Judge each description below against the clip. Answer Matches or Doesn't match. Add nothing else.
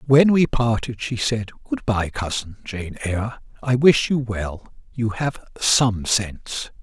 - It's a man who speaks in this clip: Matches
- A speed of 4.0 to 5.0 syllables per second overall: Doesn't match